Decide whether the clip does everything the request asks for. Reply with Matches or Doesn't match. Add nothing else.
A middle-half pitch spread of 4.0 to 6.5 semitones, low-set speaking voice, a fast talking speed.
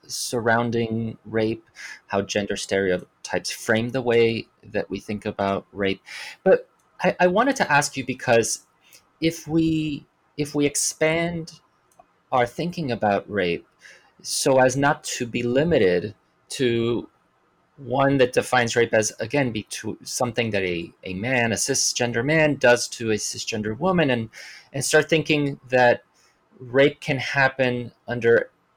Doesn't match